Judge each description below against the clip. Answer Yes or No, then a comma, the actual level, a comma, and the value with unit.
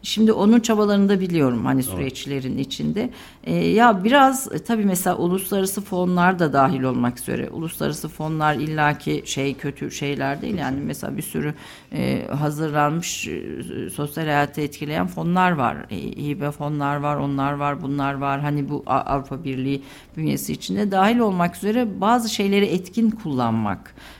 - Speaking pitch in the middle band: Yes, medium, 150 Hz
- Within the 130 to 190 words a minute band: Yes, fast, 140 wpm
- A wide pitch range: Yes, wide, 5.9 semitones